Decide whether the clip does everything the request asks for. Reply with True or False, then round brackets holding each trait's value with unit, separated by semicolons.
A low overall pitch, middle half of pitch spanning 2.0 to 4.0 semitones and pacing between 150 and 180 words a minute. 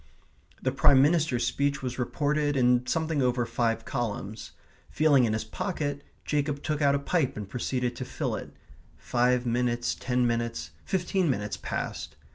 True (125 Hz; 3.2 semitones; 155 wpm)